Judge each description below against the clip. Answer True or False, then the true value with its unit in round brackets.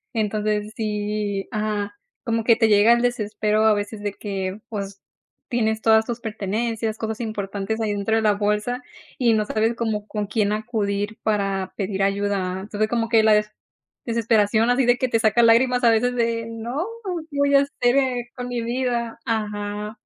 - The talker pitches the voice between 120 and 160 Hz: False (220 Hz)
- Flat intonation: True (2.1 semitones)